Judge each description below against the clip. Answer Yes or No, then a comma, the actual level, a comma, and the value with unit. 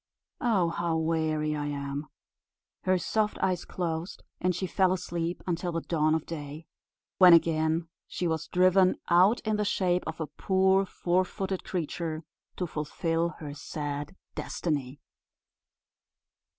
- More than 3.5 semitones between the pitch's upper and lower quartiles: No, average, 2.8 semitones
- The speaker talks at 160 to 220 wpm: No, average, 140 wpm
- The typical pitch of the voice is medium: Yes, medium, 170 Hz